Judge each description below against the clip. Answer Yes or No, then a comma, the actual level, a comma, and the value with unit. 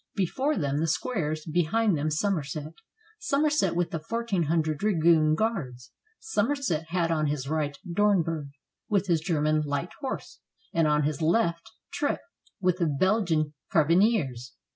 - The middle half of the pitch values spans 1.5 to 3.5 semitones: No, average, 4.9 semitones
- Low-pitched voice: No, medium, 165 Hz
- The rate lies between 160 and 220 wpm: No, average, 140 wpm